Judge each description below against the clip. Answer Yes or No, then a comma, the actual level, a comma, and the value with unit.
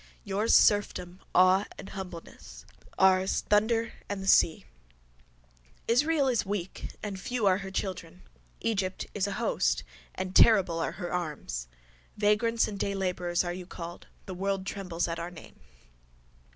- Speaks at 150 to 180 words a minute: No, average, 140 wpm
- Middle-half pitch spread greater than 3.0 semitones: No, narrow, 2.5 semitones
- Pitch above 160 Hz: Yes, high, 190 Hz